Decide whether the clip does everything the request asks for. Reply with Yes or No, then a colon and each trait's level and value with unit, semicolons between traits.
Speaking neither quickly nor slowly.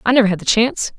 No: fast, 305 wpm